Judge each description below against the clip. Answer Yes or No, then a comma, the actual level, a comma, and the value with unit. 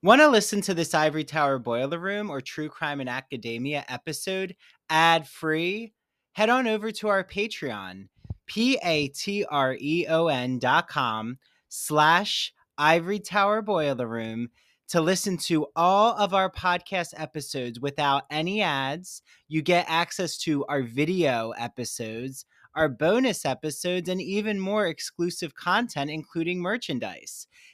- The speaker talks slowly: Yes, slow, 125 wpm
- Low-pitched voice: No, medium, 160 Hz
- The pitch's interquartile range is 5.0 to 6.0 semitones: Yes, wide, 5.6 semitones